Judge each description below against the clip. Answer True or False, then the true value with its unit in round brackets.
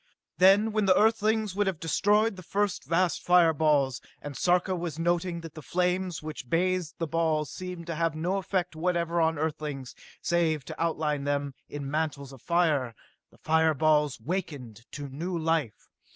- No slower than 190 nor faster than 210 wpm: False (180 wpm)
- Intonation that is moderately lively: True (3.3 semitones)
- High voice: False (165 Hz)